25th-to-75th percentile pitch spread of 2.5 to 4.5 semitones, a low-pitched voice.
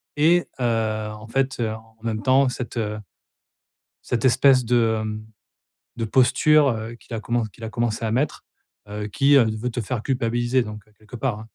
Yes: average, 2.8 semitones; low, 115 Hz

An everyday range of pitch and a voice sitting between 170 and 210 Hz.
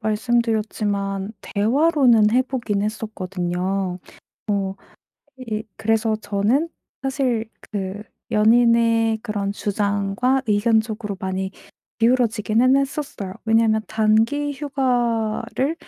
No: average, 3.0 semitones; high, 220 Hz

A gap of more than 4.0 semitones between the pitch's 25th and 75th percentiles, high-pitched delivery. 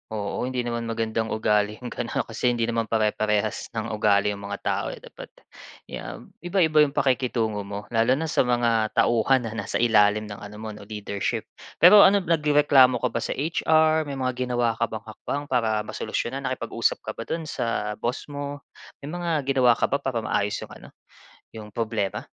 No: average, 4.4 semitones; low, 115 Hz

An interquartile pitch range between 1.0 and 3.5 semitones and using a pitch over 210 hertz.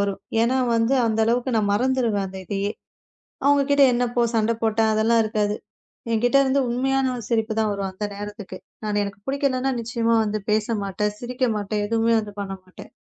Yes: average, 2.9 semitones; high, 225 Hz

